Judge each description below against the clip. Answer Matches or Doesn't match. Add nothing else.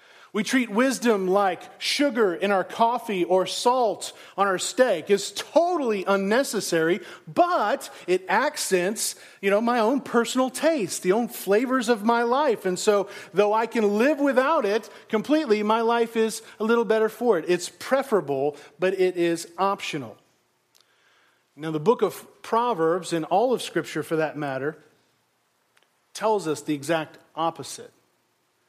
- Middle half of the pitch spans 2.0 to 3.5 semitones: Doesn't match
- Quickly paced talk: Doesn't match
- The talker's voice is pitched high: Matches